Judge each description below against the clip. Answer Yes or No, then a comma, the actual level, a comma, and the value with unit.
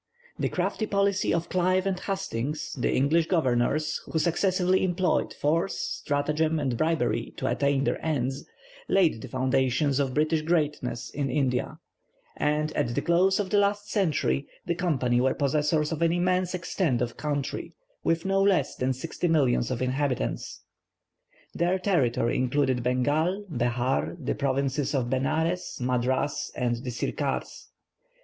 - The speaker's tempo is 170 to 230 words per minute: No, average, 145 wpm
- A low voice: No, medium, 150 Hz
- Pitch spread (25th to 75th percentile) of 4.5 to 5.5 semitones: Yes, average, 5.2 semitones